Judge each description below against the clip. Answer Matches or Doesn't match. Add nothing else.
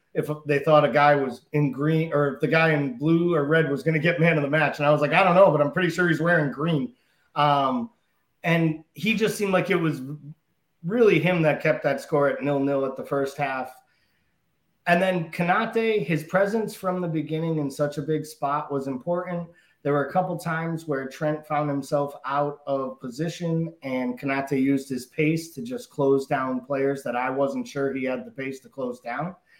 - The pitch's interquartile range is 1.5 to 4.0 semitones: Matches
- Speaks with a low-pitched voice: Doesn't match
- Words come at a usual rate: Doesn't match